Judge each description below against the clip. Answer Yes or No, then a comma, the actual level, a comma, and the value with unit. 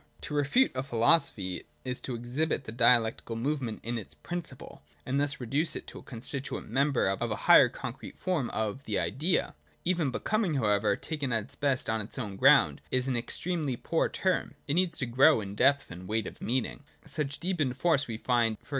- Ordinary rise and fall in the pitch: Yes, average, 4.8 semitones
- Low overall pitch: Yes, low, 130 Hz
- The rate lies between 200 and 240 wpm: Yes, fast, 205 wpm